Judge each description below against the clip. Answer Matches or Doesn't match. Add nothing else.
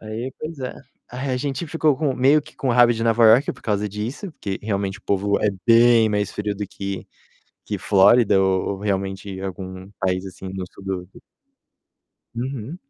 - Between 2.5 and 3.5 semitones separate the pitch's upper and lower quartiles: Doesn't match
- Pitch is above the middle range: Doesn't match